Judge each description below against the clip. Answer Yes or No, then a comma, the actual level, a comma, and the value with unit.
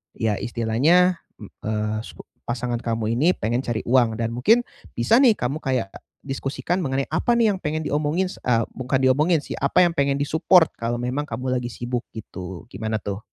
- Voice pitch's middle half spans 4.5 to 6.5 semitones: Yes, average, 4.9 semitones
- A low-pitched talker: Yes, low, 125 Hz